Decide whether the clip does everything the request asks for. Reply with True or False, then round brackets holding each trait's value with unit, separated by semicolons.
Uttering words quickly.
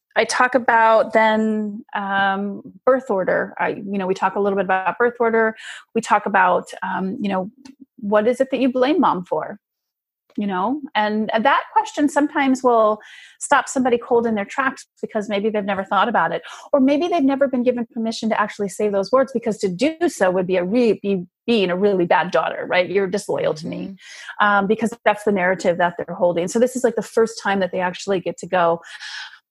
True (210 wpm)